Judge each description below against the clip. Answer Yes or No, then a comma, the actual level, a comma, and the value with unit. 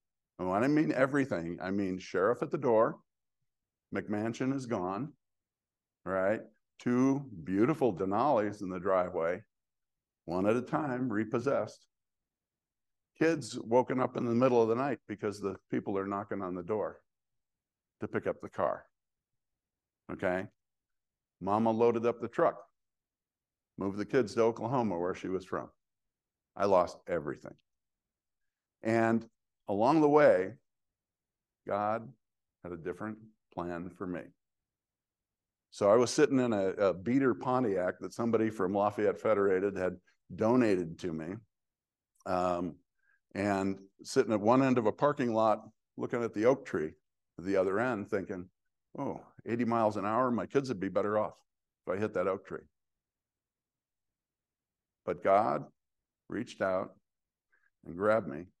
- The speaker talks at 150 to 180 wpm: No, average, 140 wpm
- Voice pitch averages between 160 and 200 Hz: No, low, 105 Hz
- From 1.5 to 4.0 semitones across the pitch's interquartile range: No, average, 4.4 semitones